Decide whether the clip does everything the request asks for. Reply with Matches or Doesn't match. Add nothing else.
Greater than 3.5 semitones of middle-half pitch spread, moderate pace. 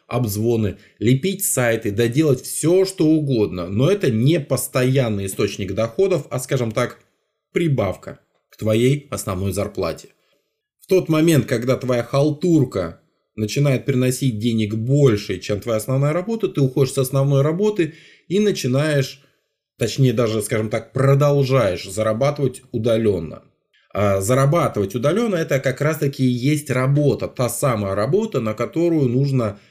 Matches